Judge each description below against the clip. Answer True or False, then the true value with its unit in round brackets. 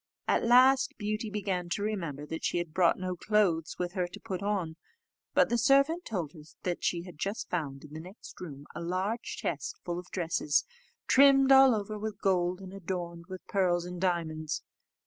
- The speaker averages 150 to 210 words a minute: True (185 wpm)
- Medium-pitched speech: True (180 Hz)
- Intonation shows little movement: False (3.8 semitones)